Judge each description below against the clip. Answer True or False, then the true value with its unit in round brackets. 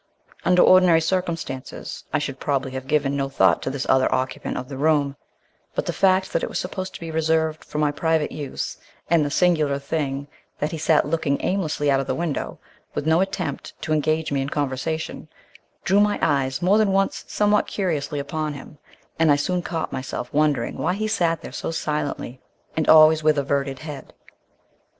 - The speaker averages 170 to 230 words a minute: True (190 wpm)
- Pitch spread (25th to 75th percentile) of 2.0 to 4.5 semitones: True (3.1 semitones)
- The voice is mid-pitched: True (155 Hz)